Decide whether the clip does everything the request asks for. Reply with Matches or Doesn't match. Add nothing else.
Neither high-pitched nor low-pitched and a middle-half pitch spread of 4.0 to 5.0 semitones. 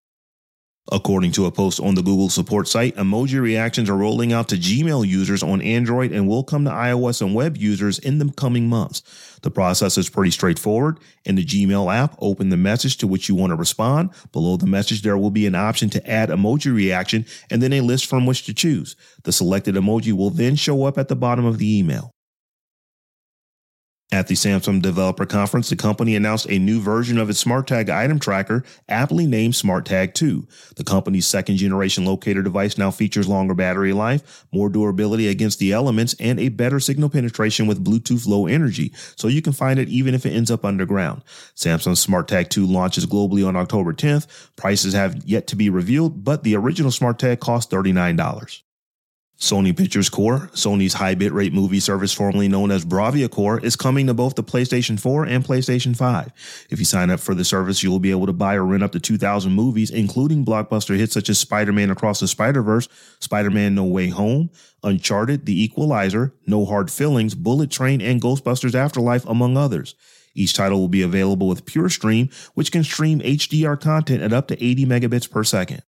Doesn't match